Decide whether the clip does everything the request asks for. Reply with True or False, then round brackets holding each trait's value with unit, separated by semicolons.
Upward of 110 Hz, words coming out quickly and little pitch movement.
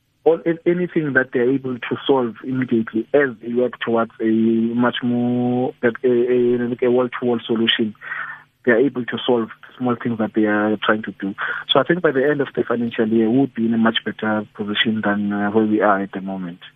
True (120 Hz; 210 wpm; 2.2 semitones)